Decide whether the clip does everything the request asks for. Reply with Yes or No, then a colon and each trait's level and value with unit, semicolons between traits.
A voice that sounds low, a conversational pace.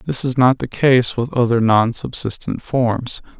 Yes: low, 125 Hz; average, 175 wpm